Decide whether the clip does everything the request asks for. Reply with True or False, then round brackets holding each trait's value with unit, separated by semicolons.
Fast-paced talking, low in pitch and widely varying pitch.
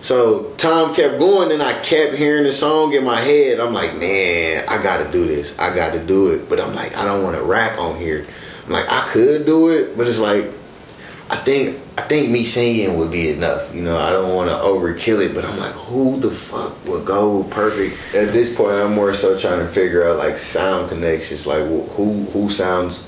True (230 wpm; 105 Hz; 8.2 semitones)